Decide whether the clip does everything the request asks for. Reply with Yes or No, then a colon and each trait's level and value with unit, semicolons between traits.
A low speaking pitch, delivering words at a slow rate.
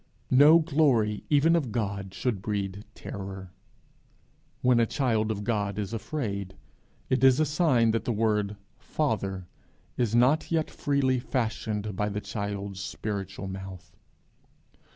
Yes: low, 110 Hz; slow, 130 wpm